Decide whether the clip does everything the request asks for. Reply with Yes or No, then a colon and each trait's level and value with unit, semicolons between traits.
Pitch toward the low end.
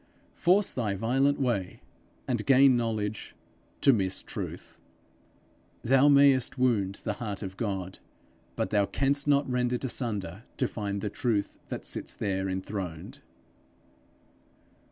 Yes: low, 115 Hz